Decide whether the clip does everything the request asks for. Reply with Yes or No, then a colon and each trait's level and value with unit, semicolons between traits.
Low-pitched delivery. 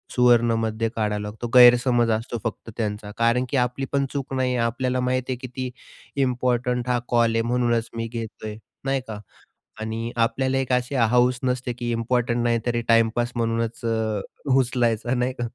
Yes: low, 120 Hz